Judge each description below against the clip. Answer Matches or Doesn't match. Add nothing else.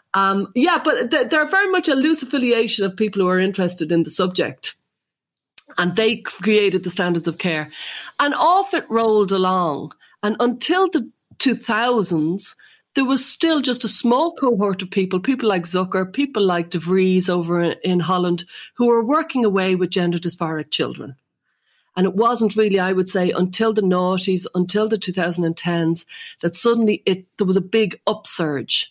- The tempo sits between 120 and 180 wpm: Matches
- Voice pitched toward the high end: Matches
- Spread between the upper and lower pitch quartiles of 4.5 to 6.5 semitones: Matches